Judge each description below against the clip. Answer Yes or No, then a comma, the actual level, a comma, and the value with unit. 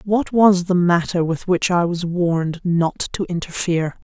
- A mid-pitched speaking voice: Yes, medium, 175 Hz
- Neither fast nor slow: Yes, average, 175 wpm